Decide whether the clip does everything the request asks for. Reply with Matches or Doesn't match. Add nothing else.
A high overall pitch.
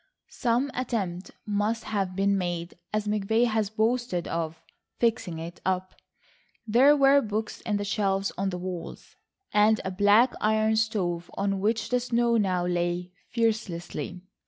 Matches